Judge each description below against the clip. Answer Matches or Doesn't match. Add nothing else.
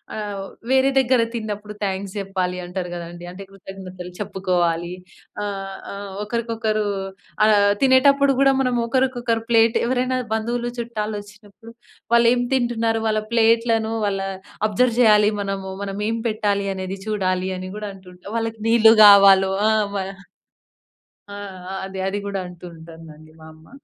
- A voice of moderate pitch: Doesn't match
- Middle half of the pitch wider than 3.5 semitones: Doesn't match